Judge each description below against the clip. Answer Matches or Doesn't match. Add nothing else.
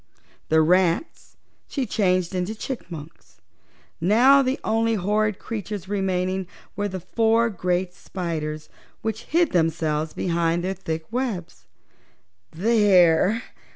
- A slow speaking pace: Matches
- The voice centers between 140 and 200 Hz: Matches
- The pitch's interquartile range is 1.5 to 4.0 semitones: Doesn't match